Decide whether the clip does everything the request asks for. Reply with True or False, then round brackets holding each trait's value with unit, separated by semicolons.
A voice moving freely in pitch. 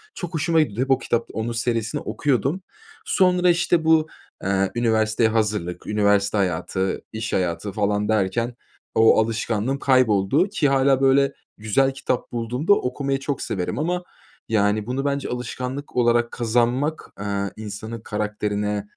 False (4.7 semitones)